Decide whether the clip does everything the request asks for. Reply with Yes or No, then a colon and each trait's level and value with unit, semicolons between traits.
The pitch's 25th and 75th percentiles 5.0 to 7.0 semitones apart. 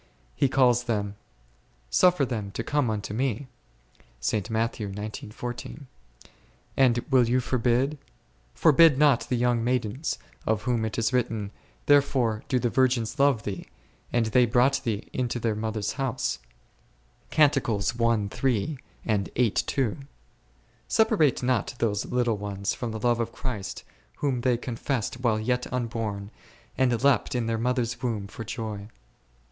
No: average, 2.8 semitones